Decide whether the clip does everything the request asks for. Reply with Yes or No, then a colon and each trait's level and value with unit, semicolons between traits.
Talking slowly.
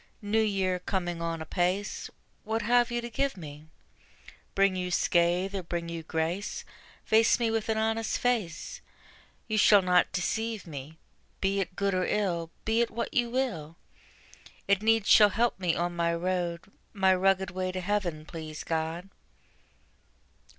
No: average, 155 wpm